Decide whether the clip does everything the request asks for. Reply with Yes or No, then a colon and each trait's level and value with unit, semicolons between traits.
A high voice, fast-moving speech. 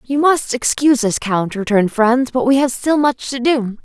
Yes: very high, 250 Hz; fast, 220 wpm